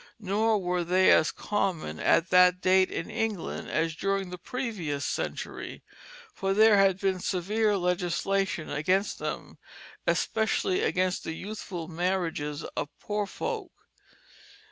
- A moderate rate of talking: No, slow, 125 wpm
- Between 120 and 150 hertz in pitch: No, medium, 185 Hz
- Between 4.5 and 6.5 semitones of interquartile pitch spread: No, average, 2.8 semitones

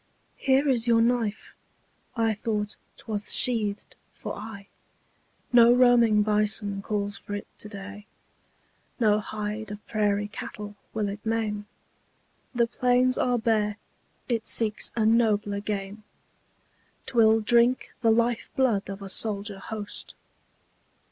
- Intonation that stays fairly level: Yes, narrow, 2.1 semitones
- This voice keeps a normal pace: No, slow, 125 wpm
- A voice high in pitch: Yes, high, 215 Hz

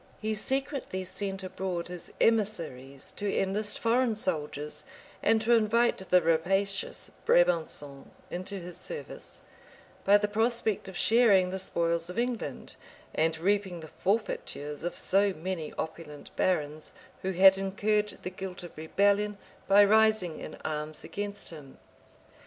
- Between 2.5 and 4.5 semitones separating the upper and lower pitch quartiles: Yes, average, 3.8 semitones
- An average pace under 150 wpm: Yes, slow, 135 wpm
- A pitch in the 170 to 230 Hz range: Yes, high, 190 Hz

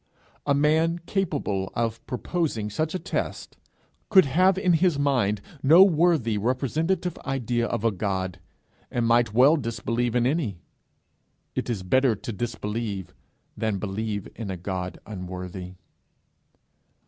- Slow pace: Yes, slow, 130 wpm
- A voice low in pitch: Yes, low, 120 Hz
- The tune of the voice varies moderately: No, wide, 6.8 semitones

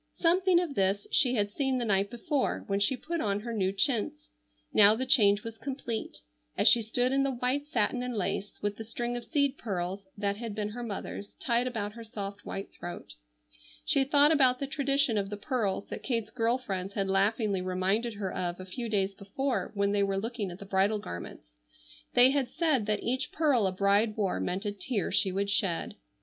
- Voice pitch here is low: No, high, 215 Hz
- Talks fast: Yes, fast, 210 wpm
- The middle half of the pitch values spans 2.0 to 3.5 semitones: No, average, 4.3 semitones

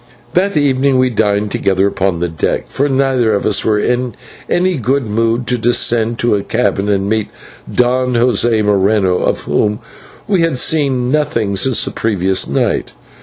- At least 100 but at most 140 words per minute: No, average, 165 wpm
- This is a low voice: Yes, low, 115 Hz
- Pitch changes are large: No, average, 3.9 semitones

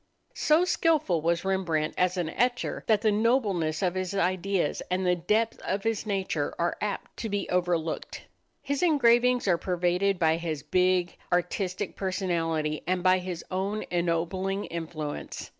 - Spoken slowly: No, average, 150 wpm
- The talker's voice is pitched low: No, medium, 185 Hz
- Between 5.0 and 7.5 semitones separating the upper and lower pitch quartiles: No, average, 3.1 semitones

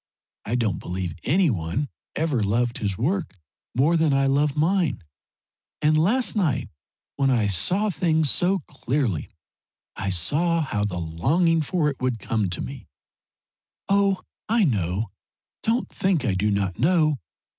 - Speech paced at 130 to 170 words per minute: Yes, average, 145 wpm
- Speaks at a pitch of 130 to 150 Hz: Yes, low, 135 Hz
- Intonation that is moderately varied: No, wide, 8.4 semitones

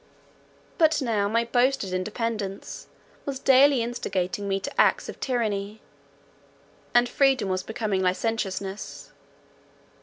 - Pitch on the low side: No, high, 220 Hz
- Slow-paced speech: Yes, slow, 110 wpm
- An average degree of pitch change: Yes, average, 3.9 semitones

